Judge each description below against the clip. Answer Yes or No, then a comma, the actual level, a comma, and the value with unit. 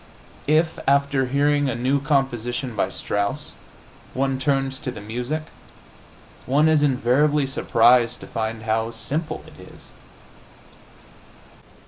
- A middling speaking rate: No, slow, 115 wpm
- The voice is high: No, low, 135 Hz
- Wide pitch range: No, average, 3.3 semitones